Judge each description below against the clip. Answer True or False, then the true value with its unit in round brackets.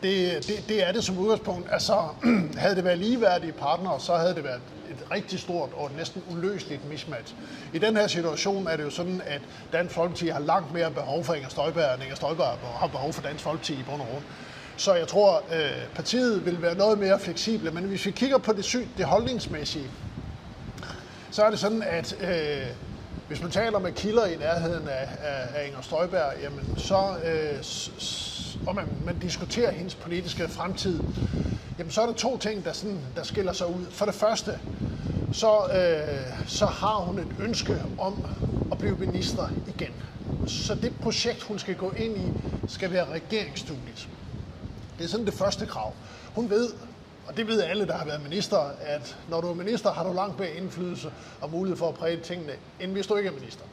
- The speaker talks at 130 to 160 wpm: False (200 wpm)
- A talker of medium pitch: True (175 Hz)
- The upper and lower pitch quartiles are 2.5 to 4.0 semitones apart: False (5.0 semitones)